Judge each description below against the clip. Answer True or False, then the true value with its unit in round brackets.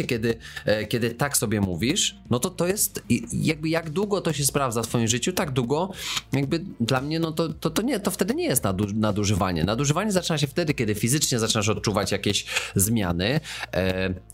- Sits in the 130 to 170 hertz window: False (120 Hz)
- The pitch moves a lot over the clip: True (6.9 semitones)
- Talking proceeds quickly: True (190 wpm)